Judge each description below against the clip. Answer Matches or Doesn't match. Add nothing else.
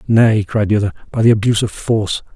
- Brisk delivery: Matches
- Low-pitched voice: Matches